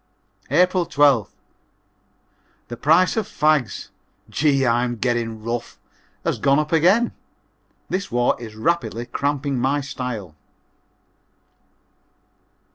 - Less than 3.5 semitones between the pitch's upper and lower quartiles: No, average, 4.4 semitones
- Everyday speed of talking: No, slow, 100 wpm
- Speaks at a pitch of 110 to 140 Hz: Yes, low, 135 Hz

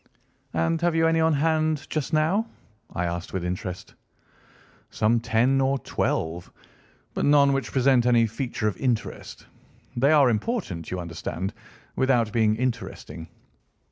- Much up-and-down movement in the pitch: Yes, wide, 7.3 semitones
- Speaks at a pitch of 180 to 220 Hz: No, low, 125 Hz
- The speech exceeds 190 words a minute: No, average, 140 wpm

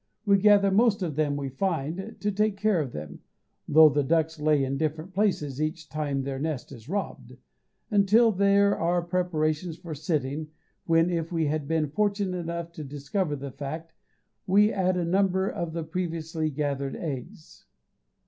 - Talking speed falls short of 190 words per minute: Yes, average, 165 wpm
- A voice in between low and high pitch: Yes, medium, 165 Hz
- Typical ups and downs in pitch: Yes, average, 4.2 semitones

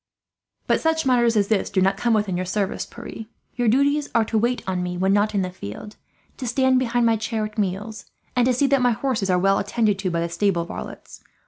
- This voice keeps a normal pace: No, fast, 235 wpm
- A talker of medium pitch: No, high, 215 Hz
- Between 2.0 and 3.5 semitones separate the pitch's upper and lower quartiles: No, average, 4.1 semitones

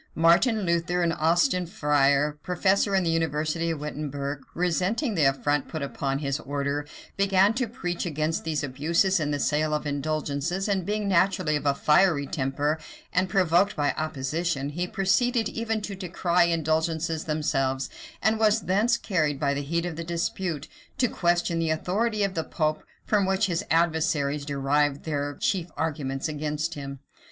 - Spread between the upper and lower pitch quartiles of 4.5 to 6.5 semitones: No, average, 4.1 semitones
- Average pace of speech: Yes, average, 160 wpm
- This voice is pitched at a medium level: Yes, medium, 160 Hz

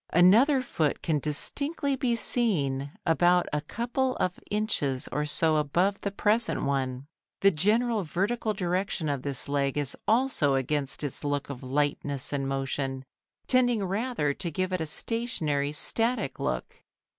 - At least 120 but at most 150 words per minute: Yes, average, 145 wpm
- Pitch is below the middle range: No, medium, 165 Hz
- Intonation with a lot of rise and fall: Yes, wide, 7.7 semitones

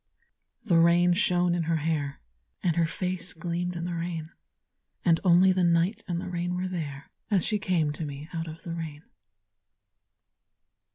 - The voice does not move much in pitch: Yes, narrow, 1.6 semitones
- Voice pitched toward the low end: No, medium, 170 Hz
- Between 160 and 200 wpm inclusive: Yes, average, 170 wpm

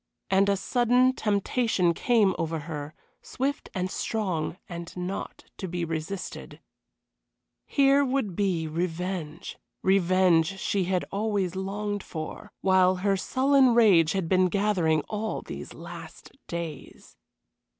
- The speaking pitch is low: No, high, 190 Hz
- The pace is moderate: No, slow, 120 wpm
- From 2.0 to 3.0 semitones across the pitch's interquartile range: No, average, 3.7 semitones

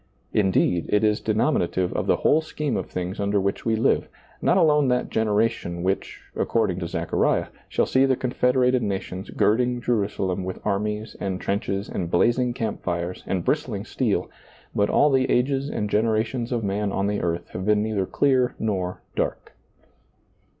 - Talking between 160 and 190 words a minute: Yes, average, 170 wpm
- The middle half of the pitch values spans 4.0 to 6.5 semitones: Yes, average, 4.4 semitones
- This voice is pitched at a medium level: No, low, 105 Hz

